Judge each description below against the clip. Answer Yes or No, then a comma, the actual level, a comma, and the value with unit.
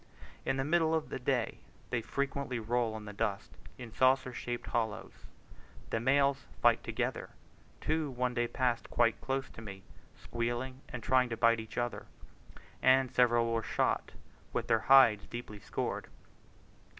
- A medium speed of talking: Yes, average, 155 wpm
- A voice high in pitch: No, low, 120 Hz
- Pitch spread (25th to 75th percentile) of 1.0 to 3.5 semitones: Yes, narrow, 2.5 semitones